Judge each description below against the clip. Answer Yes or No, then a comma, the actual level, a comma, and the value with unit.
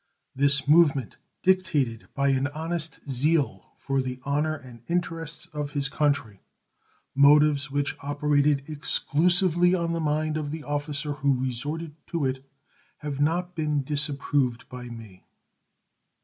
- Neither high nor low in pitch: Yes, medium, 145 Hz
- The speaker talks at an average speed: No, slow, 130 wpm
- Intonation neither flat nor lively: No, narrow, 2.3 semitones